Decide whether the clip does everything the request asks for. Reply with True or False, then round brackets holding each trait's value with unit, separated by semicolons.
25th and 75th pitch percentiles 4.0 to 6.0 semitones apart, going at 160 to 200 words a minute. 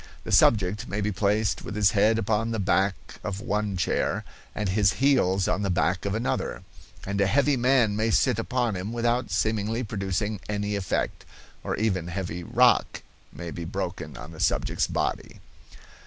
False (2.8 semitones; 170 wpm)